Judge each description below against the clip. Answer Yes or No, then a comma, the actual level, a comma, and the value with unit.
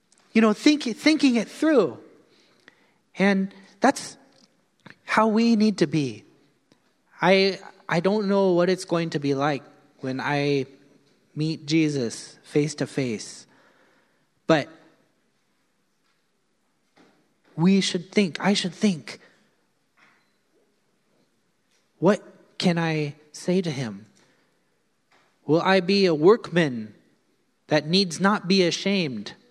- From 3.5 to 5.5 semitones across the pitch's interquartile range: Yes, average, 4.8 semitones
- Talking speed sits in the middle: No, slow, 110 wpm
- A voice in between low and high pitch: Yes, medium, 180 Hz